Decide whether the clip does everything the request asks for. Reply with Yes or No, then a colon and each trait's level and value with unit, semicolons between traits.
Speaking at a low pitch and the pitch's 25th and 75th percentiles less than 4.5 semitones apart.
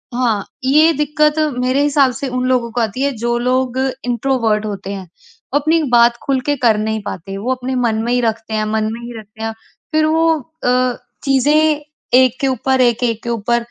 No: high, 245 Hz; average, 3.3 semitones